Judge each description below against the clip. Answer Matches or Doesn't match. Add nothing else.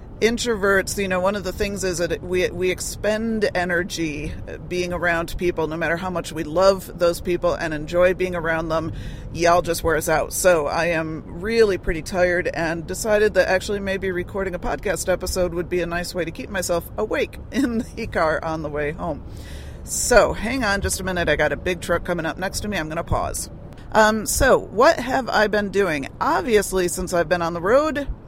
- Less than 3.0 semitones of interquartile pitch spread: Matches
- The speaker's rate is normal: Doesn't match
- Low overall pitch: Doesn't match